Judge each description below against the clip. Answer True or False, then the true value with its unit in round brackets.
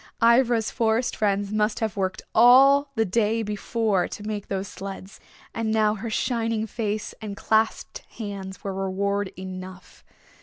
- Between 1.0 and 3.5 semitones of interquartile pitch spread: True (2.4 semitones)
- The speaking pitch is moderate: False (215 Hz)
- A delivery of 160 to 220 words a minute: False (145 wpm)